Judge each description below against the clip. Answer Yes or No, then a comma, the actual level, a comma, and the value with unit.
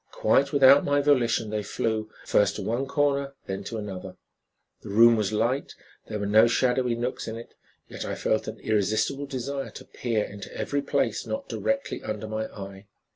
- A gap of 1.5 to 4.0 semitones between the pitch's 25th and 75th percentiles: No, average, 4.6 semitones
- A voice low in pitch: Yes, low, 115 Hz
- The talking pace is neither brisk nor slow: Yes, average, 180 wpm